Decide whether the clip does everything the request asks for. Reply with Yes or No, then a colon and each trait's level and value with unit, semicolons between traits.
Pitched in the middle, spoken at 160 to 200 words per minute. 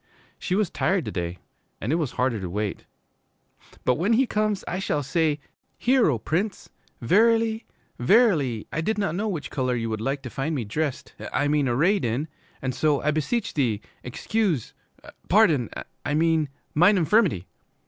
Yes: medium, 155 Hz; average, 170 wpm